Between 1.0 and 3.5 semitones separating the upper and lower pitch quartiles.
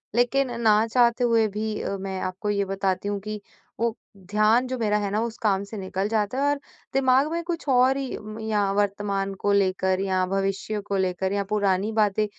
Yes: average, 2.7 semitones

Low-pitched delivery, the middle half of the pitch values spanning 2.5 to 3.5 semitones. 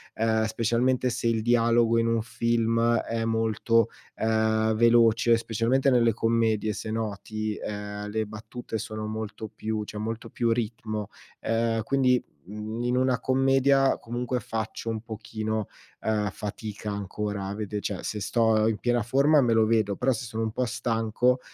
No: low, 115 Hz; narrow, 1.5 semitones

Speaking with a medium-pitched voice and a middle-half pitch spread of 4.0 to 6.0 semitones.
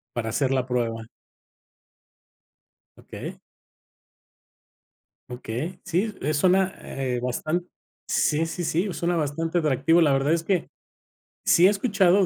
Yes: medium, 160 Hz; average, 5.1 semitones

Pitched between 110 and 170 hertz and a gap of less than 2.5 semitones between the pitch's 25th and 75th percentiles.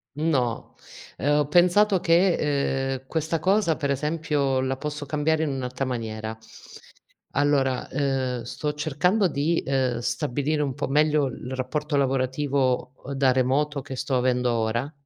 No: medium, 140 Hz; average, 2.8 semitones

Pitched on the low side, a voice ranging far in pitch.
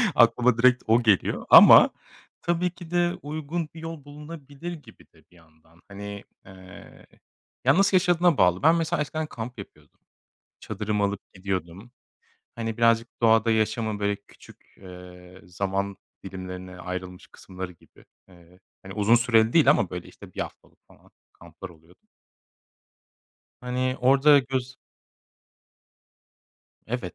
Yes: low, 110 Hz; wide, 7.2 semitones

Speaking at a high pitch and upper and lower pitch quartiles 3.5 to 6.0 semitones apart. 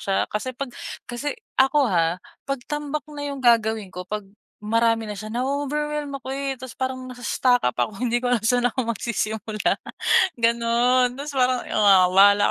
Yes: high, 245 Hz; average, 3.8 semitones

